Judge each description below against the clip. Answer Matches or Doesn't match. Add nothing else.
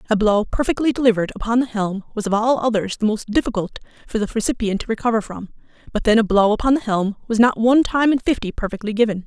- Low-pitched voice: Doesn't match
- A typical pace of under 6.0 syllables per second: Doesn't match